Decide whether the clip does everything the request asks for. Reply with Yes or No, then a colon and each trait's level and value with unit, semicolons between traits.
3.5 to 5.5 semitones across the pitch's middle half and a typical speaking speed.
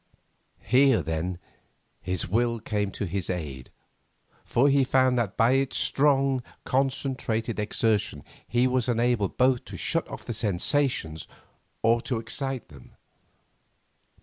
No: average, 4.8 semitones; slow, 125 wpm